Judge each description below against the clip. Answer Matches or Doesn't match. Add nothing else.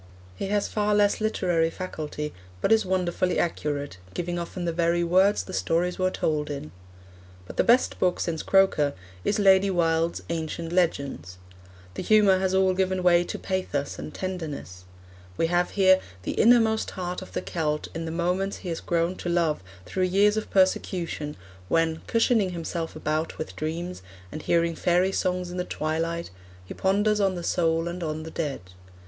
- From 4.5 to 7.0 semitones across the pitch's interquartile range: Doesn't match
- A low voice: Doesn't match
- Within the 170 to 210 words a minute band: Matches